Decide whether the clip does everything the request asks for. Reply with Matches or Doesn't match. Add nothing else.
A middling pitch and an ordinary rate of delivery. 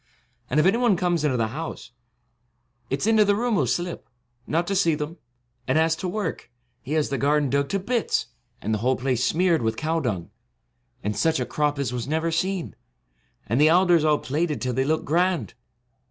Doesn't match